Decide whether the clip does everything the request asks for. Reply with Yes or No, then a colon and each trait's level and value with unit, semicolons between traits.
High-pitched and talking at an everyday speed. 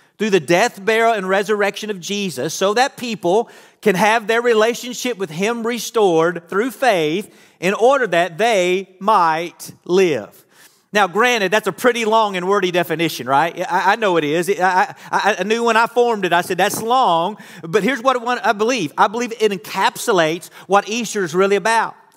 Yes: high, 205 Hz; average, 175 wpm